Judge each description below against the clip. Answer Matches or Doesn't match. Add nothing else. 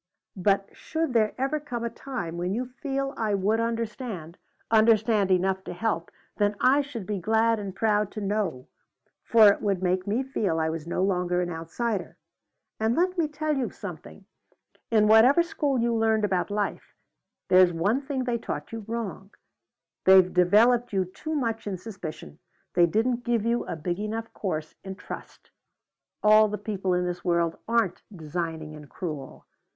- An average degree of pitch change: Matches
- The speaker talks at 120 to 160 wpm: Doesn't match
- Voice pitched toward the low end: Doesn't match